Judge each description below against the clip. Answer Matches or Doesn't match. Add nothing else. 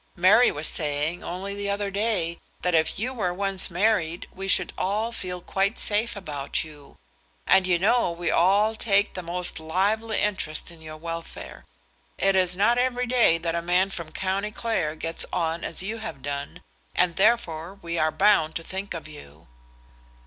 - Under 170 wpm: Doesn't match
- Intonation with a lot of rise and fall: Doesn't match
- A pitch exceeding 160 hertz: Matches